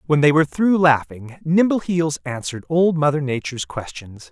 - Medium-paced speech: Yes, average, 155 wpm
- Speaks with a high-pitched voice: No, medium, 145 Hz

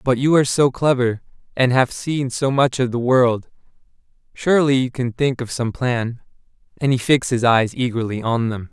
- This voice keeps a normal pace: Yes, average, 185 wpm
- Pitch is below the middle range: Yes, low, 125 Hz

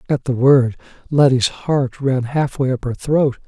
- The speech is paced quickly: No, average, 175 wpm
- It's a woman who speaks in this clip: No, male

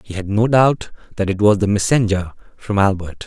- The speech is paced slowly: No, average, 200 wpm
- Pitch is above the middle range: No, low, 100 Hz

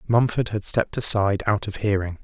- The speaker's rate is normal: Yes, average, 190 wpm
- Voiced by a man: Yes, male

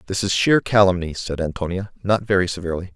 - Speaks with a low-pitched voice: Yes, very low, 95 Hz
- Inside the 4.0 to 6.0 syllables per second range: No, 6.4 syllables/s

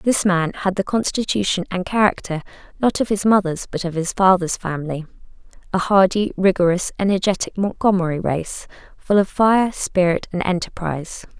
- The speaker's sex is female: Yes, female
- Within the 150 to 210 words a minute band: No, average, 140 wpm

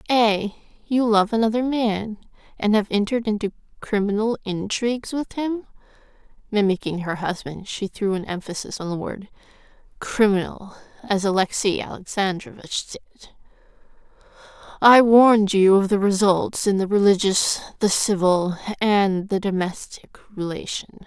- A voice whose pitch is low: No, high, 205 Hz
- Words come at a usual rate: No, slow, 120 wpm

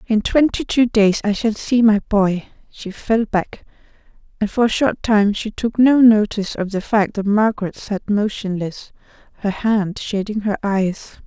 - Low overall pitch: No, high, 210 Hz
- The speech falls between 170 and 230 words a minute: Yes, average, 175 wpm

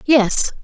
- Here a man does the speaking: No, female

